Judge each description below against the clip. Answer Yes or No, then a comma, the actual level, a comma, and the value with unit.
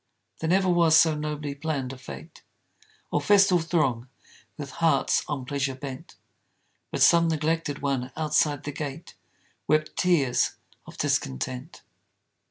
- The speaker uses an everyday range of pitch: Yes, average, 3.4 semitones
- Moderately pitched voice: Yes, medium, 150 Hz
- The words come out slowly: Yes, slow, 130 wpm